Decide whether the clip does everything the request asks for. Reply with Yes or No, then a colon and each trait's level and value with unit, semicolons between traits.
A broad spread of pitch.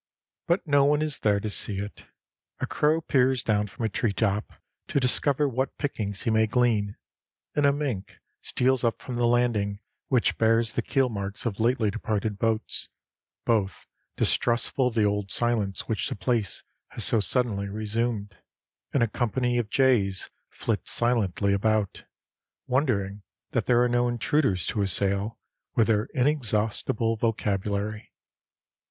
No: average, 3.3 semitones